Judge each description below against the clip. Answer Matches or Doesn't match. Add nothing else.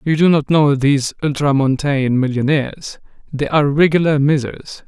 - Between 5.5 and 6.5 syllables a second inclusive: Doesn't match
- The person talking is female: Doesn't match